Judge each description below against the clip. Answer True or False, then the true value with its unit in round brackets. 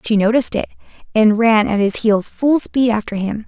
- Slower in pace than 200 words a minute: False (205 wpm)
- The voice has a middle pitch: False (220 Hz)